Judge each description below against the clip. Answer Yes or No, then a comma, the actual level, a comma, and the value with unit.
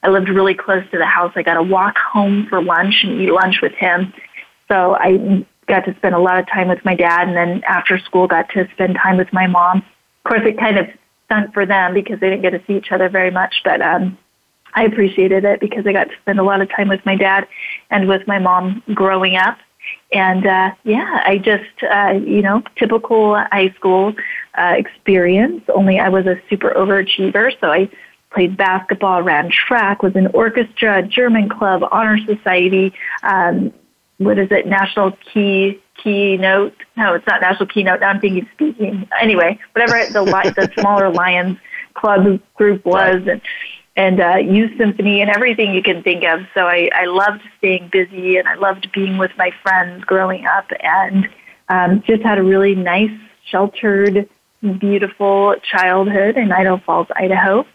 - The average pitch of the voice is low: No, high, 195 Hz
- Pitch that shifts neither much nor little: No, narrow, 1.7 semitones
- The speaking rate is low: No, average, 185 wpm